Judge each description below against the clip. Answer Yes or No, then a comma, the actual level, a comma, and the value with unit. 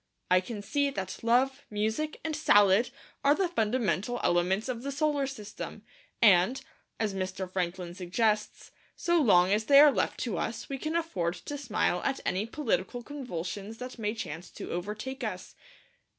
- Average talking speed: Yes, average, 165 wpm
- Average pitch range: No, wide, 6.3 semitones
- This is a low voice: No, high, 220 Hz